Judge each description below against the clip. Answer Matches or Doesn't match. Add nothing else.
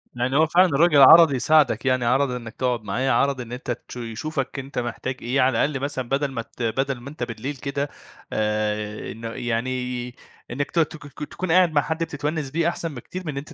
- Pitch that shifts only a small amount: Doesn't match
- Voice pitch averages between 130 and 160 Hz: Matches